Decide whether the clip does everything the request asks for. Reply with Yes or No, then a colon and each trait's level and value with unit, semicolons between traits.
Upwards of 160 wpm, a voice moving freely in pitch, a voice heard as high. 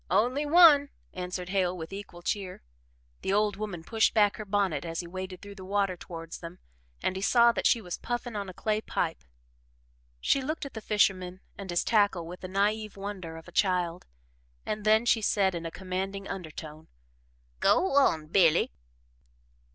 No: average, 175 wpm; average, 3.2 semitones; high, 195 Hz